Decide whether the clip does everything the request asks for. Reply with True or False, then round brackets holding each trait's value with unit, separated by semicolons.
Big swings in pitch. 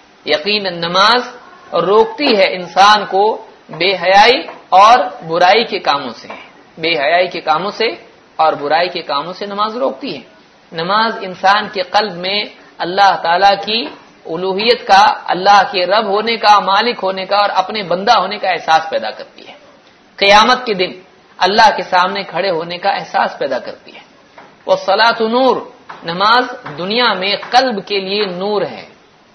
False (3.4 semitones)